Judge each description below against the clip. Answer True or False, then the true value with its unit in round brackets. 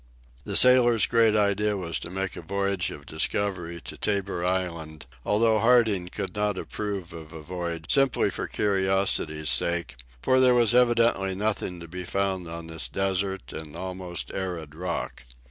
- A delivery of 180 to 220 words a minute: False (160 wpm)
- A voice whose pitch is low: True (95 Hz)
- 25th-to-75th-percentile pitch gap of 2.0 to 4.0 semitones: True (3.6 semitones)